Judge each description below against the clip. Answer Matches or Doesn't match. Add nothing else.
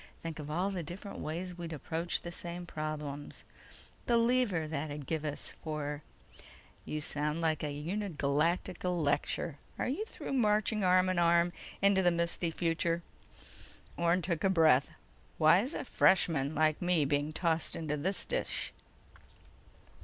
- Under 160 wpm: Matches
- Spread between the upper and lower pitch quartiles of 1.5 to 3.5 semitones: Matches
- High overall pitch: Doesn't match